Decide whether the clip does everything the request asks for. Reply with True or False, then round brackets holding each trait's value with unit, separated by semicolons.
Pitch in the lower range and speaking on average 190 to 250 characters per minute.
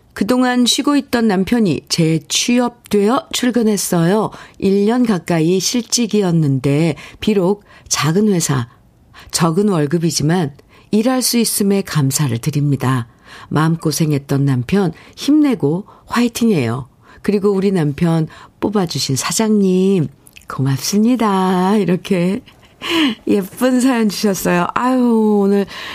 False (195 Hz; 245 characters per minute)